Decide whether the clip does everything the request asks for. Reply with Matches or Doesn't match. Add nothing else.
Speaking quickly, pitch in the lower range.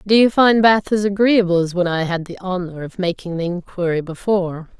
Doesn't match